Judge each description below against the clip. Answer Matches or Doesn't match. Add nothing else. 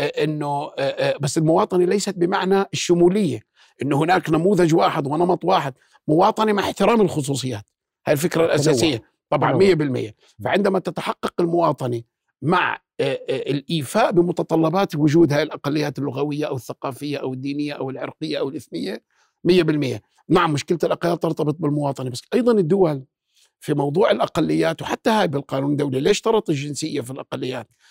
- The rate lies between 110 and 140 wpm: Matches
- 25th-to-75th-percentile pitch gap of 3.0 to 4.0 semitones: Doesn't match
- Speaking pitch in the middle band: Matches